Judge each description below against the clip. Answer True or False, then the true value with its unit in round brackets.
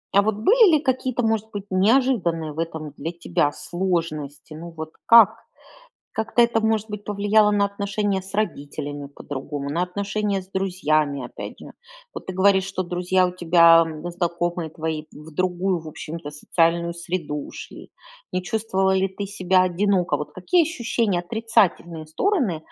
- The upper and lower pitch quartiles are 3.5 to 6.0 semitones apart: True (4.0 semitones)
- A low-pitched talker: False (185 Hz)